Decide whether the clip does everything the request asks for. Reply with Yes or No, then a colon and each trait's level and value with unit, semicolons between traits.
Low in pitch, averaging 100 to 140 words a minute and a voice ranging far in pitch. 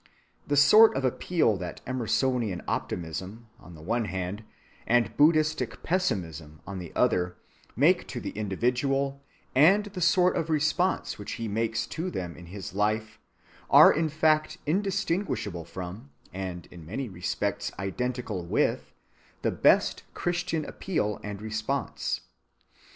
Yes: low, 115 Hz; slow, 135 wpm; wide, 8.3 semitones